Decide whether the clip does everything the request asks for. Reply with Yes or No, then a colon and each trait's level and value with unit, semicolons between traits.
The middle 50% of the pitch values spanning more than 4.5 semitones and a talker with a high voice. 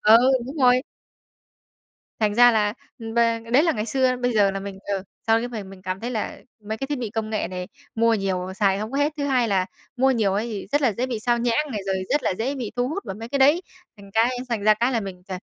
No: average, 3.8 semitones; high, 230 Hz